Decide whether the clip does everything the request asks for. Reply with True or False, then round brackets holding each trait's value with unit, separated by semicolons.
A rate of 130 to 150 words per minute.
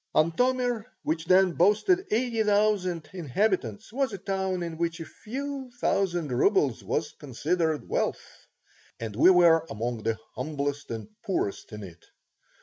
True (140 wpm)